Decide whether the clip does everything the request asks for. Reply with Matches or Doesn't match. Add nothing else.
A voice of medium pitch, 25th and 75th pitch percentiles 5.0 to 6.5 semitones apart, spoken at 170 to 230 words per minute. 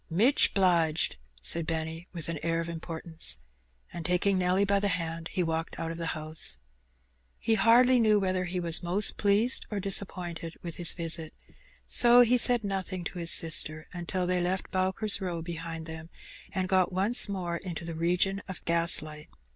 Doesn't match